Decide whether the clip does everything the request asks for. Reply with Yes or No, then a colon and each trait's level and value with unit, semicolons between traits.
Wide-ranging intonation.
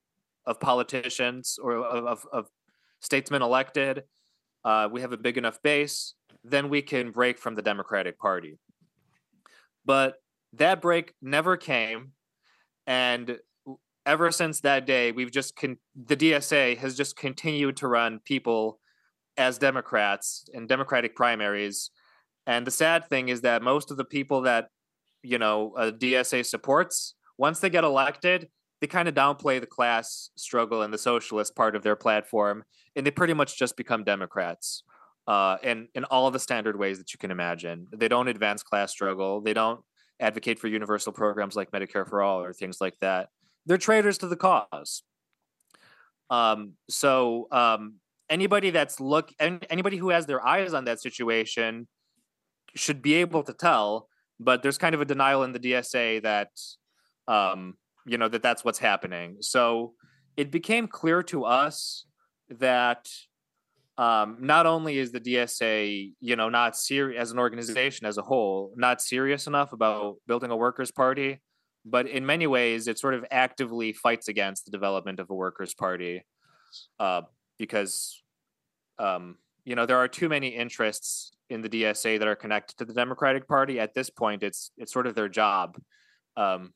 No: average, 4.2 semitones